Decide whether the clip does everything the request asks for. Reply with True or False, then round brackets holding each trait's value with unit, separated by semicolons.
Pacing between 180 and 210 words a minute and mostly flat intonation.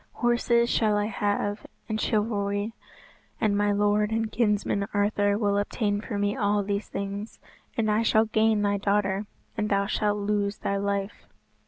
False (160 wpm; 1.2 semitones)